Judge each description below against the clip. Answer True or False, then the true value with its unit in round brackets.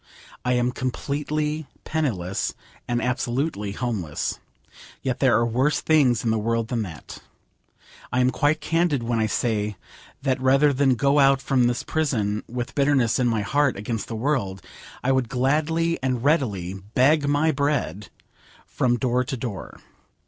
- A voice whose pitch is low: True (125 Hz)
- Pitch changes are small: False (3.9 semitones)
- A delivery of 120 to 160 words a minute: True (155 wpm)